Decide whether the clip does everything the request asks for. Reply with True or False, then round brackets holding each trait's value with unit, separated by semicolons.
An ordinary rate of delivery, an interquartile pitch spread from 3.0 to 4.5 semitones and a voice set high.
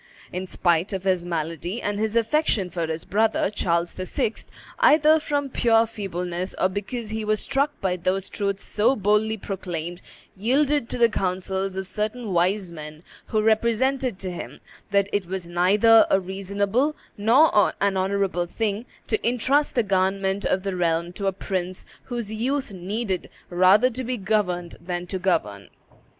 True (160 wpm; 3.7 semitones; 195 Hz)